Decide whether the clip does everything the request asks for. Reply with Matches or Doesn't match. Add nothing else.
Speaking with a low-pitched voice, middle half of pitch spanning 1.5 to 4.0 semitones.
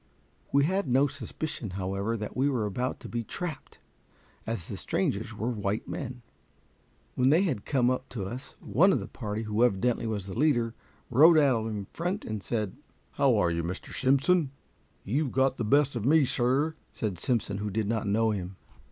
Doesn't match